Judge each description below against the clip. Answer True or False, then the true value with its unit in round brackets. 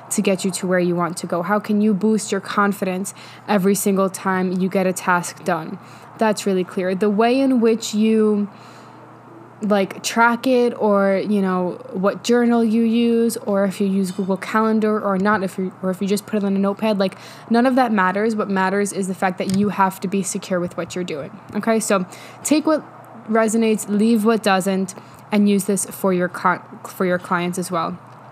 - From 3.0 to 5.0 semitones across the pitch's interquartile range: False (2.5 semitones)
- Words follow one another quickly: True (210 wpm)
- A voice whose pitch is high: True (200 Hz)